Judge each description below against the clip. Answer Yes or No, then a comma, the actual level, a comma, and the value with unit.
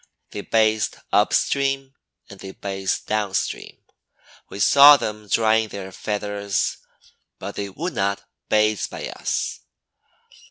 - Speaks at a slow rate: Yes, slow, 125 wpm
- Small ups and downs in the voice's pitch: Yes, narrow, 1.9 semitones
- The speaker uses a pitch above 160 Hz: No, low, 105 Hz